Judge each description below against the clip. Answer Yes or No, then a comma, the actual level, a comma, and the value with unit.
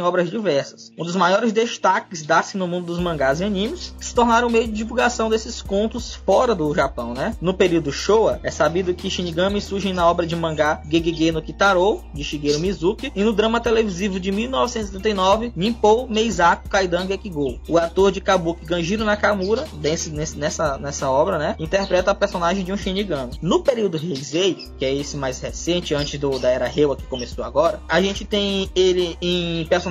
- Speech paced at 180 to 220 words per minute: Yes, fast, 185 wpm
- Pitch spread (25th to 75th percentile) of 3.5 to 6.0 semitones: Yes, average, 3.9 semitones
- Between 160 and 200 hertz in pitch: Yes, medium, 185 Hz